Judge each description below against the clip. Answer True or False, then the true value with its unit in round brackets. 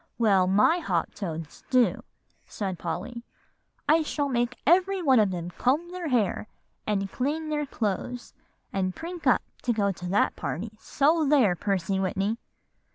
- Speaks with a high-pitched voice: True (230 Hz)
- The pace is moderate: True (155 wpm)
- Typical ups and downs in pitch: False (7.4 semitones)